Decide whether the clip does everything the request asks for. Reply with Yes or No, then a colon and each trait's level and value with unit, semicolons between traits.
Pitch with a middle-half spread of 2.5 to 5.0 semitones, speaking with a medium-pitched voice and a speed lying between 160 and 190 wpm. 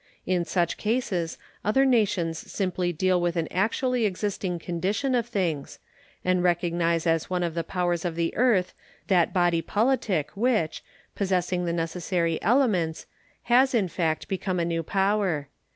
No: average, 3.5 semitones; medium, 180 Hz; average, 150 wpm